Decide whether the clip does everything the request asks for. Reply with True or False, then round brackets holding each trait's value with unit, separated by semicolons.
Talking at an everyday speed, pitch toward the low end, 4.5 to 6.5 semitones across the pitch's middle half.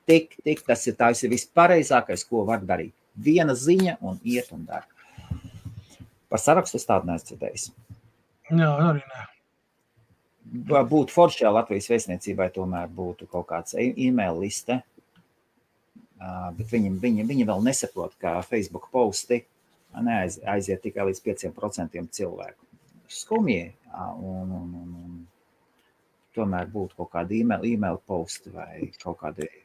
False (115 wpm; 105 Hz; 5.4 semitones)